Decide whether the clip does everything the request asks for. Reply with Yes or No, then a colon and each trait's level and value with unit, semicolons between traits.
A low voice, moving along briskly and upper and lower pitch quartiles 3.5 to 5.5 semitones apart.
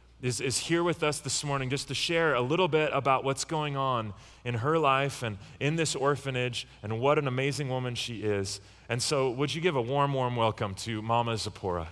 Yes: low, 130 Hz; fast, 215 wpm; average, 3.9 semitones